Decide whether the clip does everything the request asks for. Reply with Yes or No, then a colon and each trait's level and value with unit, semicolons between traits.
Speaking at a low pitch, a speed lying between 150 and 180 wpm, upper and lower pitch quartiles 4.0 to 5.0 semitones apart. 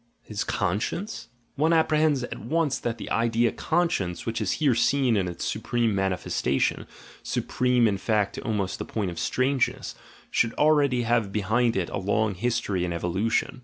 Yes: low, 115 Hz; average, 175 wpm; average, 4.6 semitones